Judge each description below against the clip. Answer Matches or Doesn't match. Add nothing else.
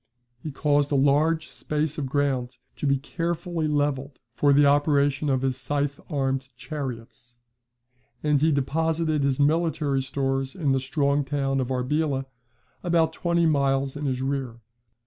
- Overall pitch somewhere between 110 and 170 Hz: Matches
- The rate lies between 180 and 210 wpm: Doesn't match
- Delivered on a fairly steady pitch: Matches